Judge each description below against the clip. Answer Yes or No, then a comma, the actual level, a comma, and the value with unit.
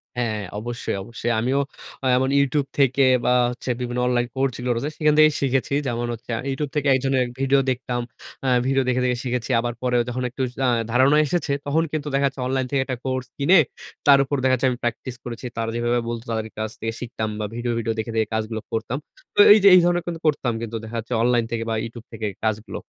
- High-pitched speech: No, low, 125 Hz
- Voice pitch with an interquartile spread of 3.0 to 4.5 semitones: No, narrow, 2.6 semitones